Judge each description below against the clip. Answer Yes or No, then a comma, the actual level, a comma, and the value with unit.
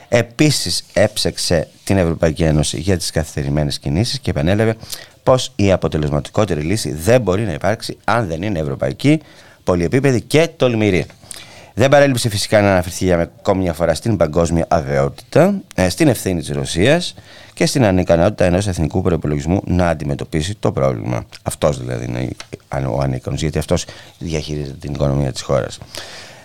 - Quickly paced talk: No, average, 145 wpm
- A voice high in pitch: No, very low, 90 Hz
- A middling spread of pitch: No, wide, 6.7 semitones